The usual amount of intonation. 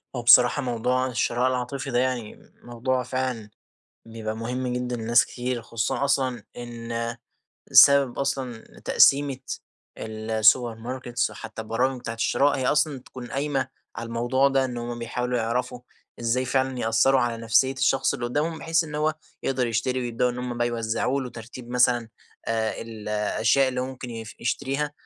No: narrow, 2.1 semitones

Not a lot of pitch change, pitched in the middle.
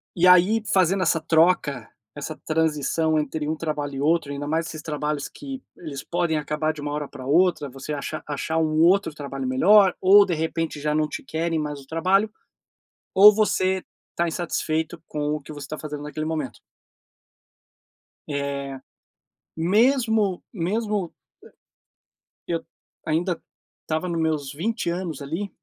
No: average, 3.4 semitones; medium, 160 Hz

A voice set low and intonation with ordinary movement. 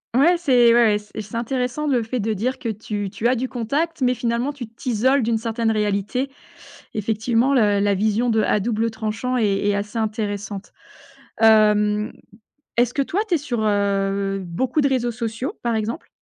No: high, 225 Hz; average, 3.1 semitones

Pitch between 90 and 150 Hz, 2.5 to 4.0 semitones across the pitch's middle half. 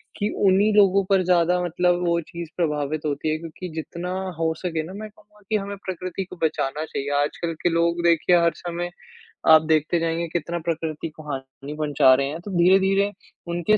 No: medium, 170 Hz; average, 2.8 semitones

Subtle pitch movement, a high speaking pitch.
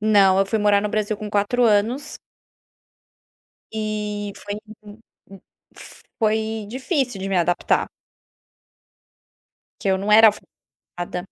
Yes: narrow, 1.5 semitones; high, 210 Hz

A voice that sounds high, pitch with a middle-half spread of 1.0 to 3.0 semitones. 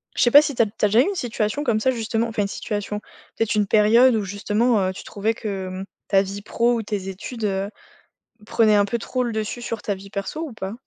Yes: high, 215 Hz; average, 2.7 semitones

